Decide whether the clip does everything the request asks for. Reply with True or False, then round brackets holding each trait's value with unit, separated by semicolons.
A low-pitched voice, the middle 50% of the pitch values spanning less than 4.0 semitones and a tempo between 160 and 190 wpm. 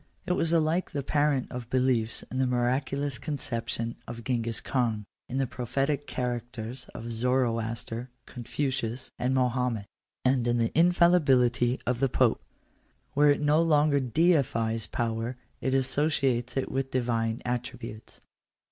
False (125 Hz; 2.9 semitones; 140 wpm)